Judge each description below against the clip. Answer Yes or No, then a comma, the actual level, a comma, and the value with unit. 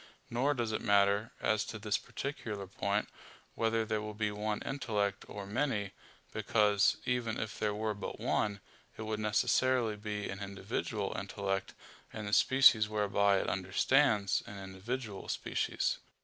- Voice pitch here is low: Yes, low, 105 Hz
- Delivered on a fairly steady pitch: Yes, narrow, 1.9 semitones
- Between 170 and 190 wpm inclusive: No, average, 145 wpm